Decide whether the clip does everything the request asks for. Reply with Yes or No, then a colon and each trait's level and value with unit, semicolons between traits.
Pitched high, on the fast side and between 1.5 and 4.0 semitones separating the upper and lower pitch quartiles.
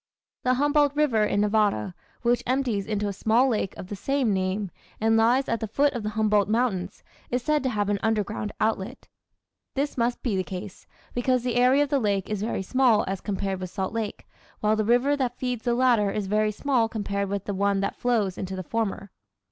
Yes: high, 220 Hz; fast, 210 wpm; average, 3.7 semitones